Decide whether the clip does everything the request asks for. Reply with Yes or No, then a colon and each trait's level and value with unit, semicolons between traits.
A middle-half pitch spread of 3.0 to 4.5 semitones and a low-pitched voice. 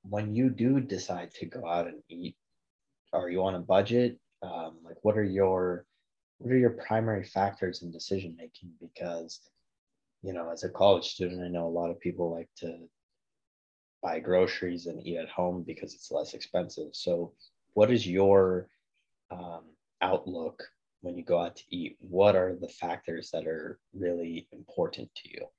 Yes: average, 3.5 semitones; very low, 90 Hz